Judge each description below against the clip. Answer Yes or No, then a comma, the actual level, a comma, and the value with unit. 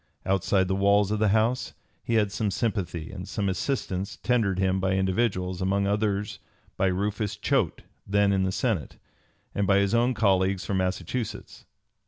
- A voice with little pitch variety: Yes, narrow, 2.0 semitones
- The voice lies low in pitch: Yes, low, 100 Hz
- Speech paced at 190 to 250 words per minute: No, average, 165 wpm